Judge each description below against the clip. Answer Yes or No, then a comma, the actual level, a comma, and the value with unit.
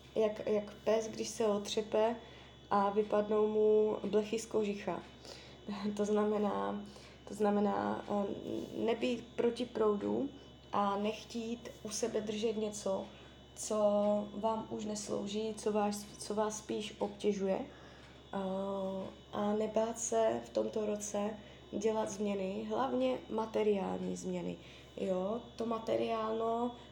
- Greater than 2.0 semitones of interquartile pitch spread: No, narrow, 1.5 semitones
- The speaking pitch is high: Yes, high, 210 Hz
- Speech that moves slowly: Yes, slow, 110 wpm